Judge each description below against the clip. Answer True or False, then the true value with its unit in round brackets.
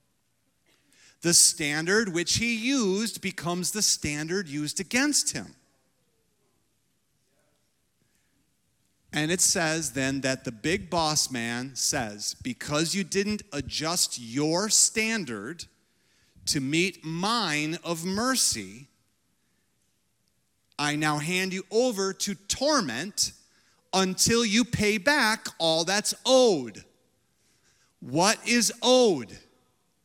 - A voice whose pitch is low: False (180 Hz)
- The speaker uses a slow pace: True (100 wpm)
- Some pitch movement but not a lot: False (6.2 semitones)